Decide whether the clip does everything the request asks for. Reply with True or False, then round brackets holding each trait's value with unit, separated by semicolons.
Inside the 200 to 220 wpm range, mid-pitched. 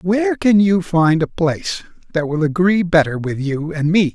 True (205 wpm; 170 Hz)